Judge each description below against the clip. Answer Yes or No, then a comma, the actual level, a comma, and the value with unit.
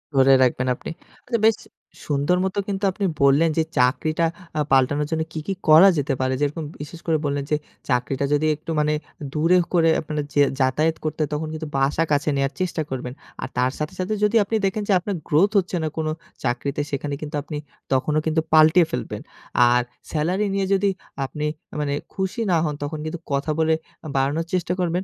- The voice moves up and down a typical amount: Yes, average, 3.5 semitones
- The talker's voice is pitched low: No, medium, 155 Hz